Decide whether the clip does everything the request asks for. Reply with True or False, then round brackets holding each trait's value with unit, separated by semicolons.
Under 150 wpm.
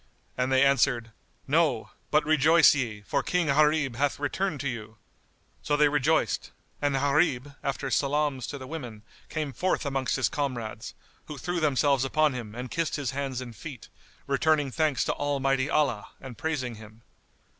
False (165 wpm)